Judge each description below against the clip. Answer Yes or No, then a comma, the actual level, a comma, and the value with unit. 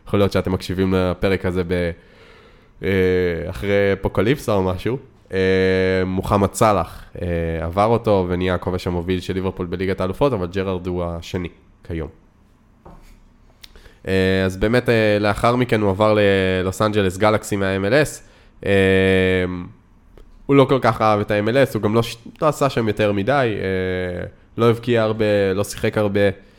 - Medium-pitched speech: No, low, 100 Hz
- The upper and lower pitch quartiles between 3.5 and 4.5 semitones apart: No, average, 2.7 semitones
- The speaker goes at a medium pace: Yes, average, 130 wpm